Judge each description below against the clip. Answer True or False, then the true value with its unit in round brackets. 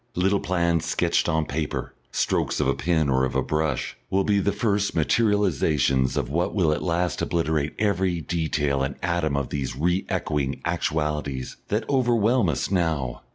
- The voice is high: False (80 Hz)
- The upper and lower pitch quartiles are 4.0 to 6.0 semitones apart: True (4.7 semitones)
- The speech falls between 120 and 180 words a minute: True (165 wpm)